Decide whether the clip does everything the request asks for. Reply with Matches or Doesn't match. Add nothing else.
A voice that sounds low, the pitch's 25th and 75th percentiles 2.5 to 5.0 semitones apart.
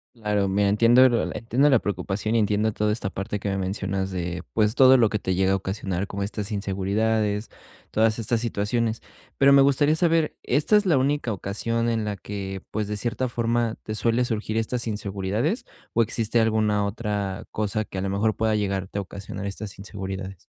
Matches